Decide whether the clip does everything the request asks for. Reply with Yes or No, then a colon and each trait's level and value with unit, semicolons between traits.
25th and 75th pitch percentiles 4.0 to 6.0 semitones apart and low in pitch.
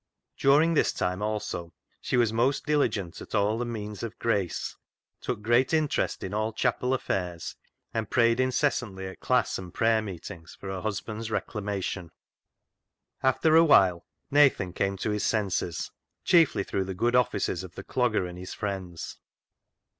Yes: average, 4.5 semitones; low, 105 Hz